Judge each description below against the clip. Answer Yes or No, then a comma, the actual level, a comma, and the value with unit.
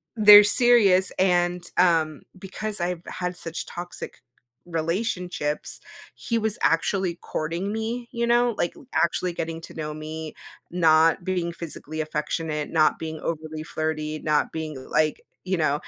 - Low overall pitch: No, medium, 170 Hz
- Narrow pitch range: No, average, 3.1 semitones